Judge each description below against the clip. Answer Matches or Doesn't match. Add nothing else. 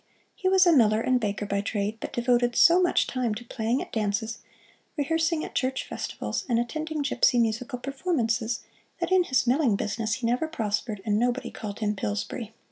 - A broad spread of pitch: Doesn't match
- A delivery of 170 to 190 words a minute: Matches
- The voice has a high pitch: Matches